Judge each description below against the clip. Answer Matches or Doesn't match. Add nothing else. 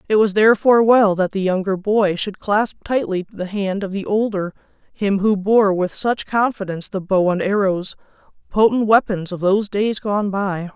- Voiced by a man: Doesn't match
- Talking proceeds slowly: Doesn't match